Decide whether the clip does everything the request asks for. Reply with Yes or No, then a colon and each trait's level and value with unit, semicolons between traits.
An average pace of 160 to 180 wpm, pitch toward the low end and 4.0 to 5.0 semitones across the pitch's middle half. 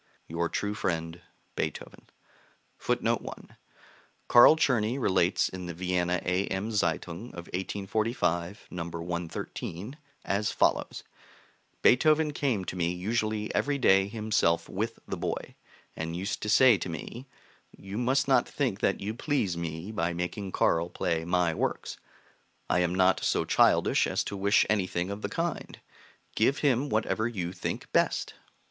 No: average, 145 wpm; very low, 95 Hz; average, 4.4 semitones